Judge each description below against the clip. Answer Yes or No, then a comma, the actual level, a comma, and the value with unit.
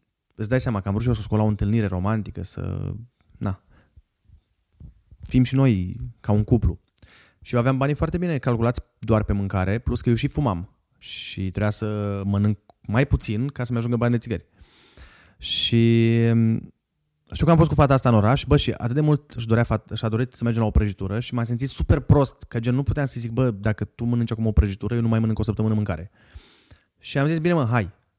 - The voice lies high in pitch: No, low, 110 Hz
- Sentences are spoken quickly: Yes, fast, 220 wpm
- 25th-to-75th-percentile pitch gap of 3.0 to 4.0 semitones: Yes, average, 3.4 semitones